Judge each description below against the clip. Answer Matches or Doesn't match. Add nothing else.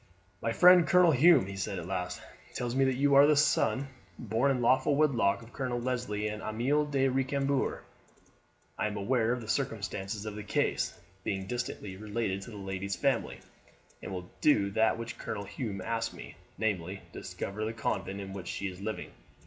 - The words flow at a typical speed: Matches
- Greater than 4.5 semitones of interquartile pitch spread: Matches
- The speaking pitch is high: Doesn't match